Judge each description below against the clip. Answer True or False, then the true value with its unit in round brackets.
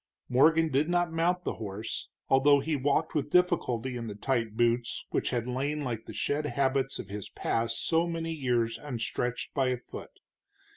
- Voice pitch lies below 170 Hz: True (135 Hz)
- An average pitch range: True (4.7 semitones)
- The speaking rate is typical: True (180 wpm)